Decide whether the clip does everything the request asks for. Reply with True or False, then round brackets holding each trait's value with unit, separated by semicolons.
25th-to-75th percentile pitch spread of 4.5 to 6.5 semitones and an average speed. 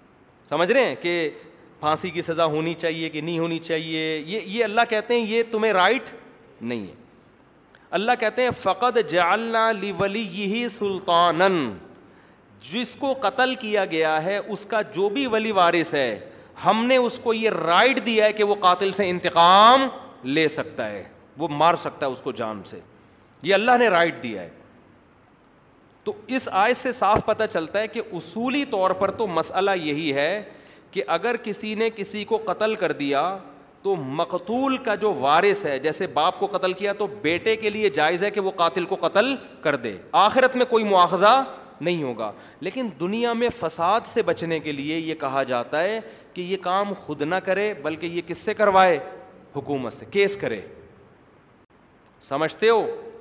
True (5.2 semitones; 180 wpm)